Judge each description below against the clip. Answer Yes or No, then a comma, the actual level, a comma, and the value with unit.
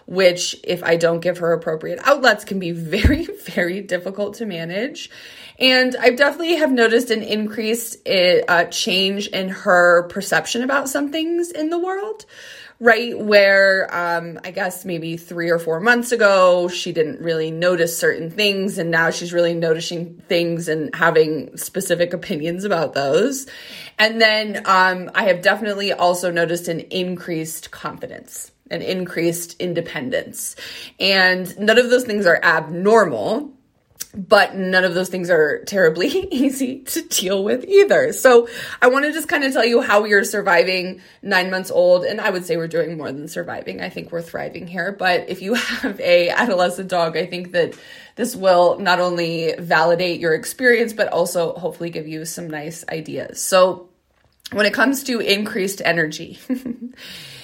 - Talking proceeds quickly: No, average, 165 wpm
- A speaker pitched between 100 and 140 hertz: No, high, 190 Hz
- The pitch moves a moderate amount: No, wide, 5.8 semitones